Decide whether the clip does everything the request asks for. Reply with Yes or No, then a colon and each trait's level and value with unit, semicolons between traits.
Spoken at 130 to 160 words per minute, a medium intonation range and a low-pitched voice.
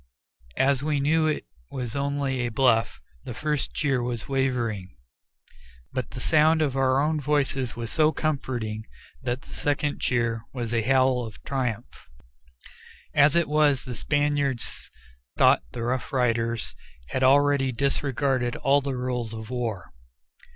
Yes: average, 145 wpm; average, 3.1 semitones; low, 130 Hz